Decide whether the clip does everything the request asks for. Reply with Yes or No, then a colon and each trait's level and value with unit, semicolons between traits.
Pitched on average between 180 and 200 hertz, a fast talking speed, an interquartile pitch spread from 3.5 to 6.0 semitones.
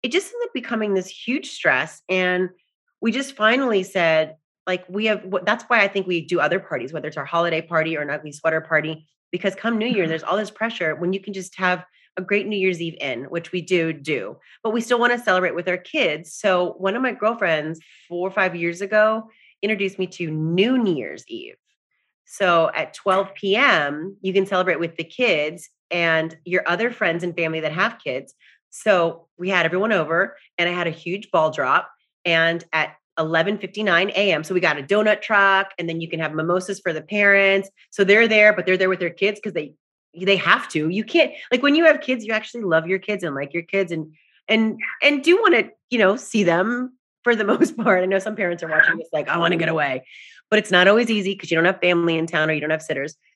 Yes: medium, 185 Hz; fast, 235 wpm; average, 4.3 semitones